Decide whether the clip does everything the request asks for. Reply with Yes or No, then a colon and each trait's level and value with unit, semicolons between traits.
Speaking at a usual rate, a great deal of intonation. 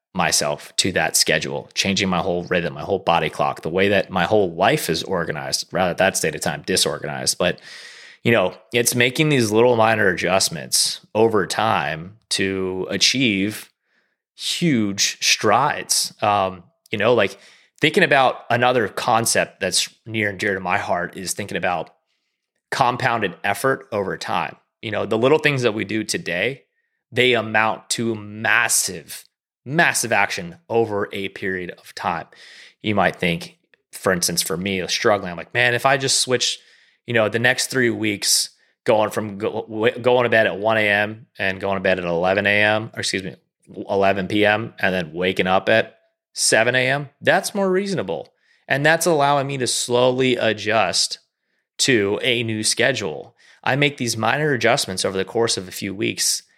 No: average, 170 wpm; average, 4.1 semitones